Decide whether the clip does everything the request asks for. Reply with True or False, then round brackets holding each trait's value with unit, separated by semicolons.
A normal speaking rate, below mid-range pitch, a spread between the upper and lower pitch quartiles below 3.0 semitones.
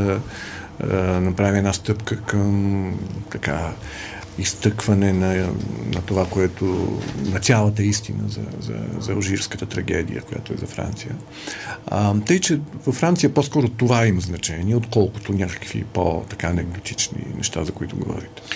True (130 wpm; 100 Hz; 2.5 semitones)